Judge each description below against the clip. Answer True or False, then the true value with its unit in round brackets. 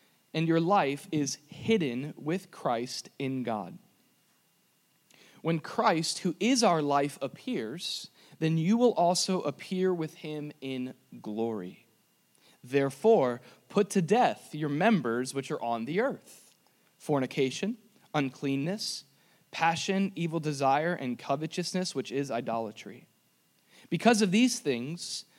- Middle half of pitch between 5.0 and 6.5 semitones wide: True (5.5 semitones)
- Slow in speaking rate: True (120 wpm)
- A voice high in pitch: False (155 Hz)